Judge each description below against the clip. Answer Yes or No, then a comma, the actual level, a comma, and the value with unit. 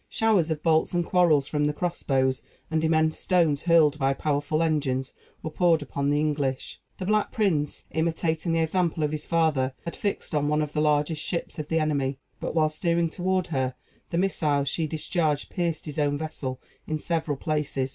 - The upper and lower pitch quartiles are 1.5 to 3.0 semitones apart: Yes, narrow, 2.4 semitones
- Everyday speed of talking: Yes, average, 190 wpm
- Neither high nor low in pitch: Yes, medium, 155 Hz